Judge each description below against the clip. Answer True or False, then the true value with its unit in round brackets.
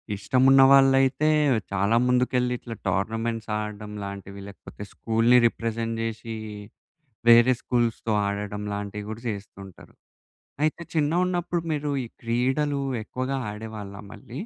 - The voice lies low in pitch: True (115 Hz)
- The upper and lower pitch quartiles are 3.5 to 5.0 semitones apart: True (4.1 semitones)